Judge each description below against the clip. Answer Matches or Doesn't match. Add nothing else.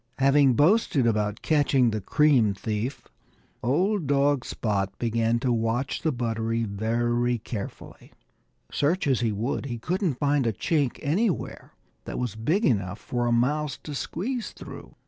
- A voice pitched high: Doesn't match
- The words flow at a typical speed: Matches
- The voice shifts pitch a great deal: Doesn't match